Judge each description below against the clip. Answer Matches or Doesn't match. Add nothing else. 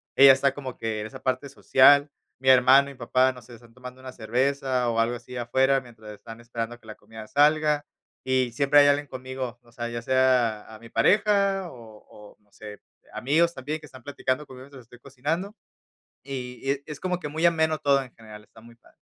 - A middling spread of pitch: Matches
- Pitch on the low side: Matches